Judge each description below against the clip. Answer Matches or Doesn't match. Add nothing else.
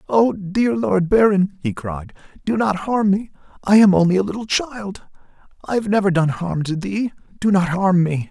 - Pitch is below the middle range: Doesn't match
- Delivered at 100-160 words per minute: Doesn't match